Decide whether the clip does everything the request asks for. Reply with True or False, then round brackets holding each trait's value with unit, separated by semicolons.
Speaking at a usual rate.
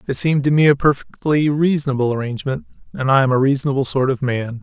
False (210 wpm)